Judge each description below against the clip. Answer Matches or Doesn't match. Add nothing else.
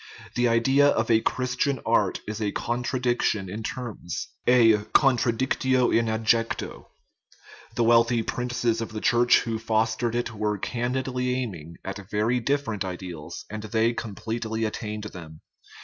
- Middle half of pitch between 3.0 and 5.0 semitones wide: Doesn't match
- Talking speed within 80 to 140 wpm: Matches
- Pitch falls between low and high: Doesn't match